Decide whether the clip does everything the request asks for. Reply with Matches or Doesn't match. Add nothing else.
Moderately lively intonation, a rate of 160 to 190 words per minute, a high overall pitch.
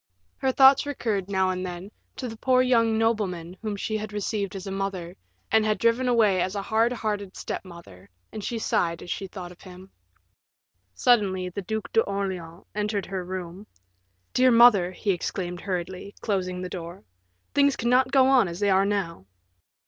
Matches